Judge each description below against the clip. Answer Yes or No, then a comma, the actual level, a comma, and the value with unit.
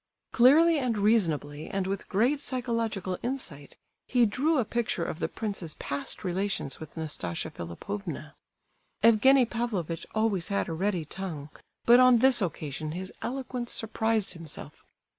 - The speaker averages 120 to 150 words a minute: Yes, average, 140 wpm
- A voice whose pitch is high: Yes, high, 205 Hz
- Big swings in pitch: Yes, wide, 6.3 semitones